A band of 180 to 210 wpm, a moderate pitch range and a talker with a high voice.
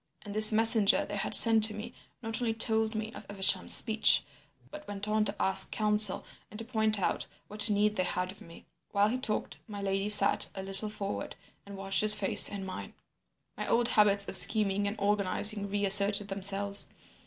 No: average, 190 wpm; narrow, 1.5 semitones; high, 205 Hz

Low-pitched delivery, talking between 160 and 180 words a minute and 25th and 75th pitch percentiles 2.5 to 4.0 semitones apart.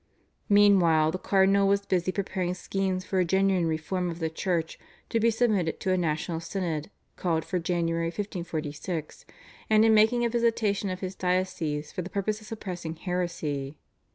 No: medium, 185 Hz; average, 165 wpm; average, 3.2 semitones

